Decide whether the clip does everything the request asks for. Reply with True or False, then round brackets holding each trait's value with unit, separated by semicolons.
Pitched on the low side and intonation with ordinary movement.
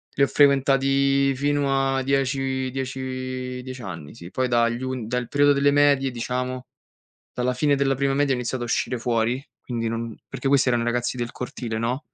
False (130 Hz; 2.1 semitones)